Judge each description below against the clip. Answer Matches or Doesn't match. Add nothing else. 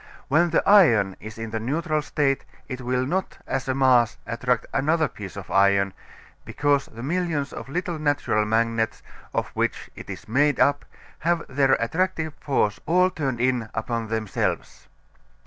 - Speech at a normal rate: Matches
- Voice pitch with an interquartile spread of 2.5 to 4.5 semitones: Doesn't match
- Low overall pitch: Matches